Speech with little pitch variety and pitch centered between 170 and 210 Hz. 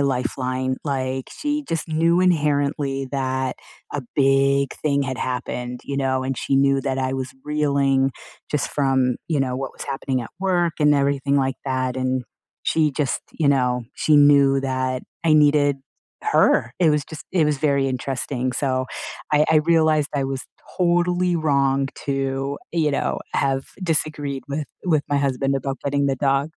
No: narrow, 2.1 semitones; medium, 140 Hz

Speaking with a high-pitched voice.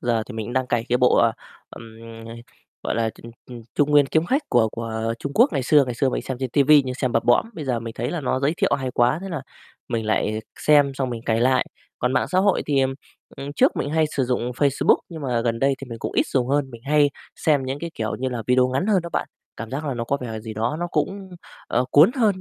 No: low, 130 Hz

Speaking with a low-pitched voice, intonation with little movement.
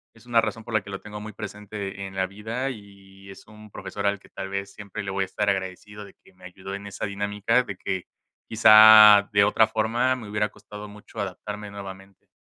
Yes: low, 105 Hz; narrow, 1.6 semitones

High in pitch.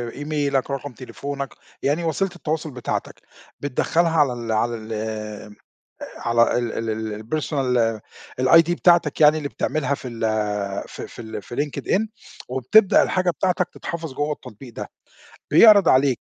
No: medium, 140 Hz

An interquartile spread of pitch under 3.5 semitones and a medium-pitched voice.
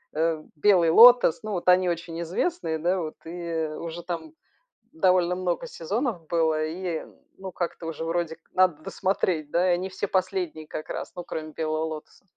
Yes: narrow, 2.5 semitones; medium, 175 Hz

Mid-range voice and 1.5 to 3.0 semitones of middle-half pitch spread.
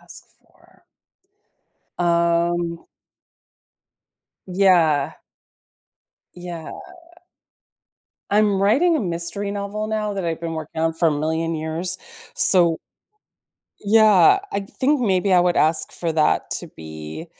No: medium, 175 Hz; average, 3.6 semitones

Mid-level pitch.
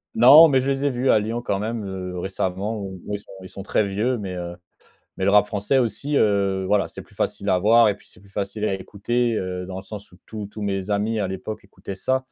No: low, 105 Hz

